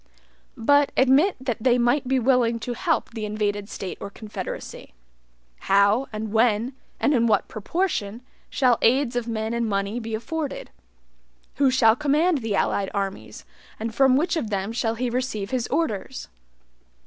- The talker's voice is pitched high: Yes, high, 235 Hz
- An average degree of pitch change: Yes, average, 3.7 semitones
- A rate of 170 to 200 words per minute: No, average, 160 wpm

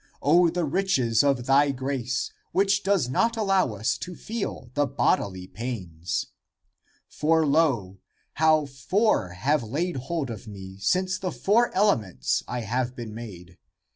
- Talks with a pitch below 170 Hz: Yes, low, 135 Hz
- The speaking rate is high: No, average, 145 wpm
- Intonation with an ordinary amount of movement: No, wide, 7.8 semitones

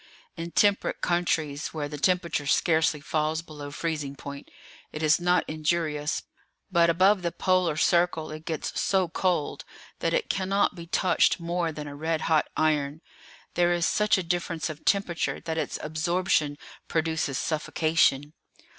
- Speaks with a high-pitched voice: No, medium, 160 Hz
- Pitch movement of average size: No, narrow, 2.3 semitones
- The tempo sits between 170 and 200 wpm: No, average, 150 wpm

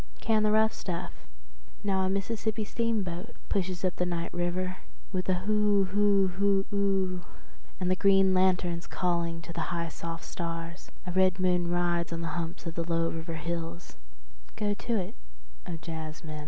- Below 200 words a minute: Yes, average, 170 wpm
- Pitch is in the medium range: Yes, medium, 180 Hz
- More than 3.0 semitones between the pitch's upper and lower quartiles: No, narrow, 2.5 semitones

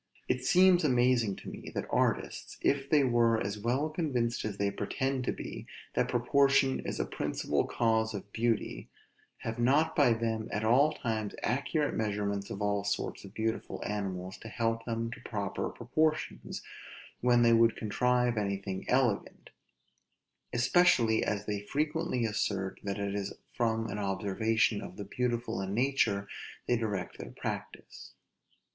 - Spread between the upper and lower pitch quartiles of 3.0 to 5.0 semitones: Yes, average, 3.5 semitones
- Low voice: Yes, low, 115 Hz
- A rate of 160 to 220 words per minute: No, average, 150 wpm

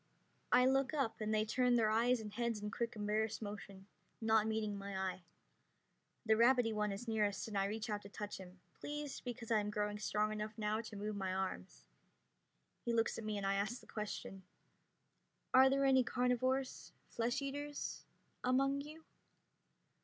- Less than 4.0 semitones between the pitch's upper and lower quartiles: Yes, average, 3.1 semitones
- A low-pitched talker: No, high, 220 Hz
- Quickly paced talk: No, average, 175 wpm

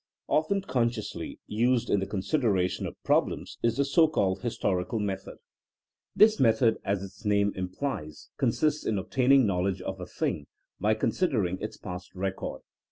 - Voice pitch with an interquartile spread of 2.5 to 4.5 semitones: No, average, 5.3 semitones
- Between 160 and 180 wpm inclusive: No, average, 150 wpm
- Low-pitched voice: Yes, low, 105 Hz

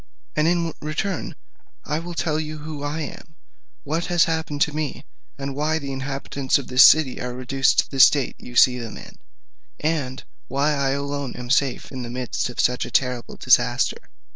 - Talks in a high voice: No, medium, 140 Hz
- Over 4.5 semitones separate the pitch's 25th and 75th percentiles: No, average, 3.2 semitones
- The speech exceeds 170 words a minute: Yes, average, 180 wpm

